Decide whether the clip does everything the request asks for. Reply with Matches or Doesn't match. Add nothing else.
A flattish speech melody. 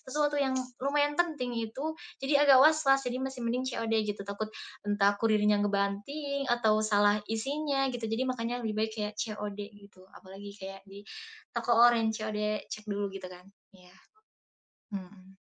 Doesn't match